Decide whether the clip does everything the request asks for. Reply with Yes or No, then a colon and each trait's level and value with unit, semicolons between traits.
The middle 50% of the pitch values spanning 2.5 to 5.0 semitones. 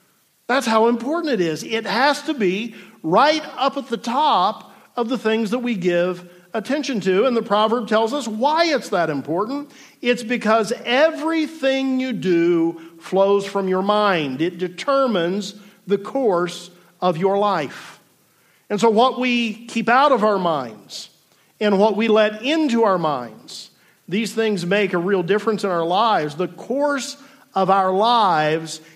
No: wide, 5.6 semitones